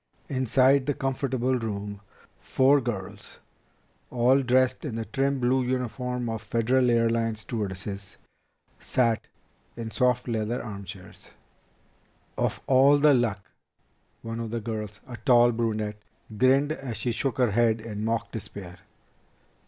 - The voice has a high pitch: No, low, 120 Hz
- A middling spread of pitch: Yes, average, 3.0 semitones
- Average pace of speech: No, slow, 130 wpm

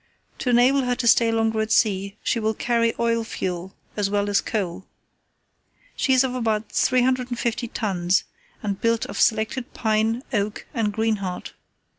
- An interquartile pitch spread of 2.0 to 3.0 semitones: Yes, average, 2.7 semitones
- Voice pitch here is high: Yes, high, 225 Hz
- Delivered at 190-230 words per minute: No, average, 155 wpm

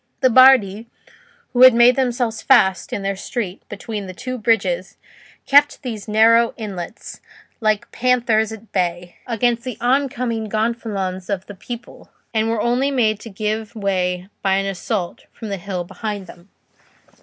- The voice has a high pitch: Yes, high, 220 Hz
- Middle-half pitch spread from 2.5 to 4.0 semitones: Yes, average, 3.5 semitones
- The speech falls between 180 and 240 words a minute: No, average, 155 wpm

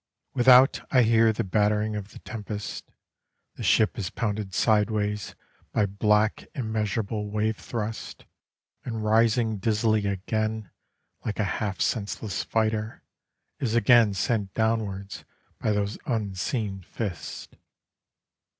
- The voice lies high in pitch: No, low, 110 Hz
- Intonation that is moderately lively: No, narrow, 1.5 semitones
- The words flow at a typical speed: No, slow, 115 wpm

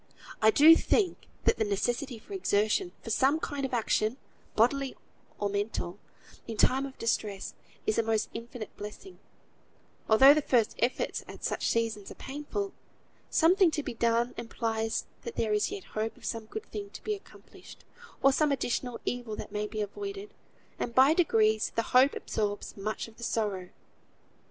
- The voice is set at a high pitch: Yes, high, 235 Hz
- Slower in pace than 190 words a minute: Yes, average, 170 wpm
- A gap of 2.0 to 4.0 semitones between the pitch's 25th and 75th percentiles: No, average, 4.7 semitones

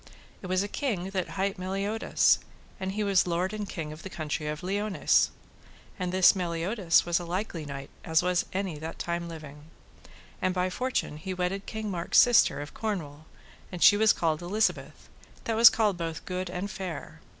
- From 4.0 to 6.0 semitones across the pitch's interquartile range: No, average, 3.1 semitones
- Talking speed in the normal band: Yes, average, 185 wpm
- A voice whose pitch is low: No, medium, 185 Hz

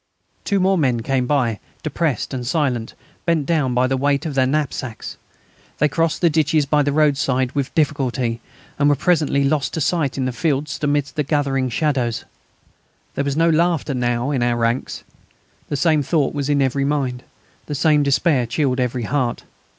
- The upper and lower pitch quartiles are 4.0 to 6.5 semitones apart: No, average, 3.0 semitones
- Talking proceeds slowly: No, average, 180 wpm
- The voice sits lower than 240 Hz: Yes, medium, 140 Hz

